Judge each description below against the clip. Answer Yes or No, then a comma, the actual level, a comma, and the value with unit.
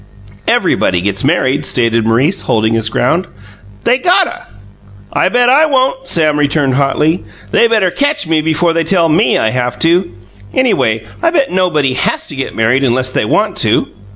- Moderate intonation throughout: No, wide, 7.7 semitones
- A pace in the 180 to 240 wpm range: No, average, 170 wpm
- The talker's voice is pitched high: No, medium, 155 Hz